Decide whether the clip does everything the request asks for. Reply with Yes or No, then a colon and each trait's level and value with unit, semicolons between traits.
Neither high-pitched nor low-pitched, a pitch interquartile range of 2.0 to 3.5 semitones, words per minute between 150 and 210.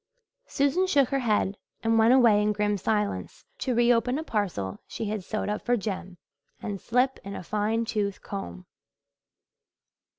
No: high, 215 Hz; average, 3.1 semitones; average, 165 wpm